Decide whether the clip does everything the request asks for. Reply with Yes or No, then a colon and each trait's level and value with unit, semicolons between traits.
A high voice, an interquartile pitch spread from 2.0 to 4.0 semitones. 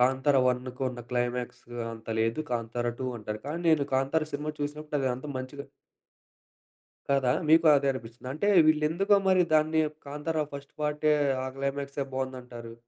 No: medium, 140 Hz; average, 3.4 semitones